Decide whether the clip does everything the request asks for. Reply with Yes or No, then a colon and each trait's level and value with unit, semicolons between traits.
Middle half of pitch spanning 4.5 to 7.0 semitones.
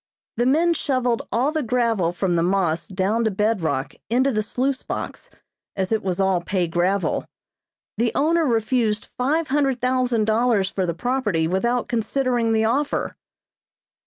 Yes: average, 4.9 semitones